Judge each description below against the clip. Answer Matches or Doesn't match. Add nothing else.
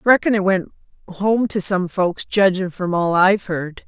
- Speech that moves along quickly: Doesn't match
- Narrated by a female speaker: Matches